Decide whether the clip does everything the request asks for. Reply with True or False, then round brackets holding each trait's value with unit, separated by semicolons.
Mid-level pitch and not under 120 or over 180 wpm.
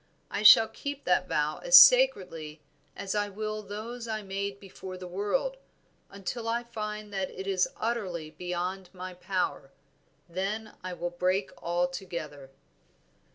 False (195 Hz; 145 wpm)